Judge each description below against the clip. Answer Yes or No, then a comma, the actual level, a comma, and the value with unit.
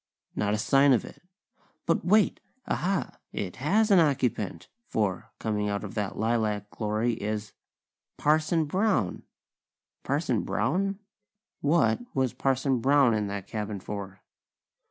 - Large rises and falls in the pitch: Yes, wide, 6.0 semitones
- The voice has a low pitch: Yes, low, 115 Hz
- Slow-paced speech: Yes, slow, 130 wpm